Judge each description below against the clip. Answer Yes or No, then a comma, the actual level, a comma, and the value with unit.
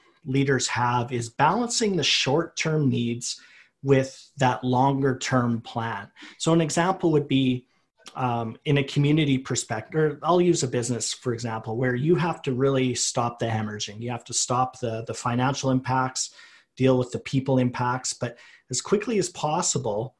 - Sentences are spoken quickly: No, average, 165 wpm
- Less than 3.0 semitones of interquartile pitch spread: Yes, narrow, 2.6 semitones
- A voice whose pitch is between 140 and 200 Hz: No, low, 130 Hz